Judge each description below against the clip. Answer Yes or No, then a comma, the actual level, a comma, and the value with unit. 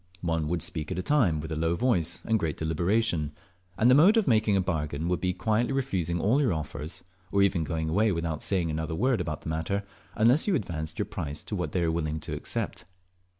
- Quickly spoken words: Yes, fast, 225 wpm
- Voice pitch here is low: Yes, very low, 85 Hz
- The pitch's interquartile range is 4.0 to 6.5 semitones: Yes, wide, 5.5 semitones